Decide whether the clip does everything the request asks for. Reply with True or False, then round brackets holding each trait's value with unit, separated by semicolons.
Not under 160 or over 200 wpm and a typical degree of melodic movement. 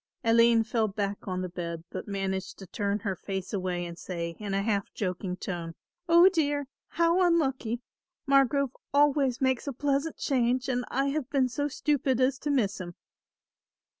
False (170 wpm; 6.3 semitones)